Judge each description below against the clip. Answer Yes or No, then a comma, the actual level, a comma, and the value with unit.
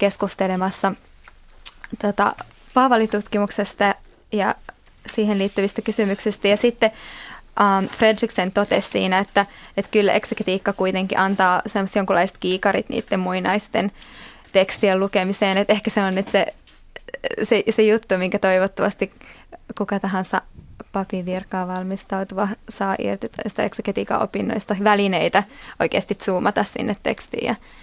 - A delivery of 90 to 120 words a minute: Yes, average, 110 wpm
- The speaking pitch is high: Yes, high, 200 Hz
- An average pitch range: No, narrow, 2.0 semitones